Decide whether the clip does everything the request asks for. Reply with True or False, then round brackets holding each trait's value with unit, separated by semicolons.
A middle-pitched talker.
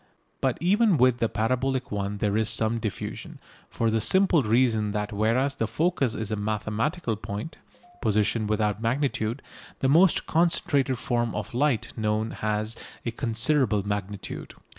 False (115 Hz)